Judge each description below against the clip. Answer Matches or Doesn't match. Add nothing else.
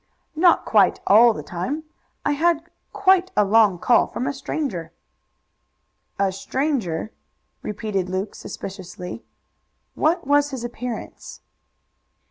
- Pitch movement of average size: Doesn't match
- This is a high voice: Matches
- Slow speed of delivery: Matches